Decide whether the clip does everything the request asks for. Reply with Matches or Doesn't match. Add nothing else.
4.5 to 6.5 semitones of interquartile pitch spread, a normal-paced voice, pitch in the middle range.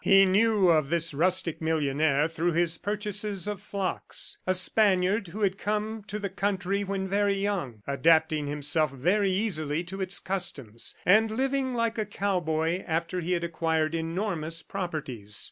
Doesn't match